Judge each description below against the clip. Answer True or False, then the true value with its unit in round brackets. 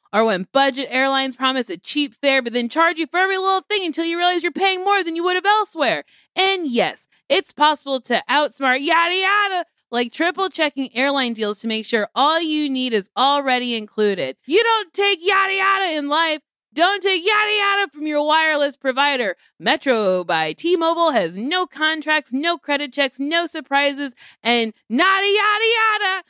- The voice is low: False (310 Hz)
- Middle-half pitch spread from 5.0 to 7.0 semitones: True (5.6 semitones)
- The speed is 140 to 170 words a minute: False (180 wpm)